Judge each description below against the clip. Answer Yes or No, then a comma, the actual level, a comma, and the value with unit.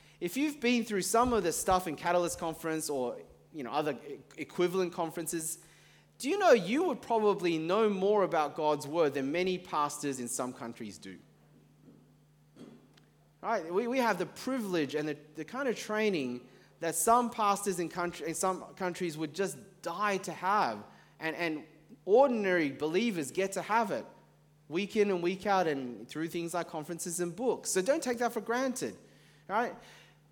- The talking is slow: No, average, 170 wpm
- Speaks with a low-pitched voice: No, medium, 175 Hz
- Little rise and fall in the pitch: No, average, 5.2 semitones